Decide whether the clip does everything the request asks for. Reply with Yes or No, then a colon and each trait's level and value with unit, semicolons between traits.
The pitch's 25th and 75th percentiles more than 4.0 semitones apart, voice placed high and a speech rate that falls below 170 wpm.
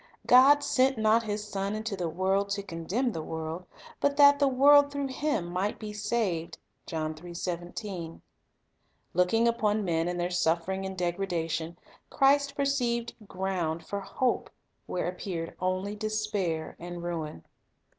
Yes: average, 5.3 semitones; high, 195 Hz; slow, 135 wpm